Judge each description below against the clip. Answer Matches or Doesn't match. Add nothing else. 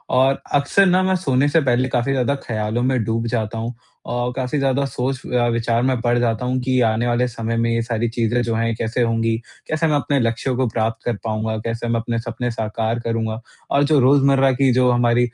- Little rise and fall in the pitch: Matches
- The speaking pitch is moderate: Doesn't match